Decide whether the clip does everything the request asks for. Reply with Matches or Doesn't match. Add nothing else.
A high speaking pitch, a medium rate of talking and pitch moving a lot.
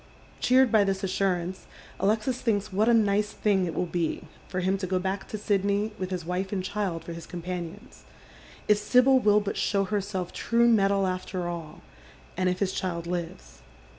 Doesn't match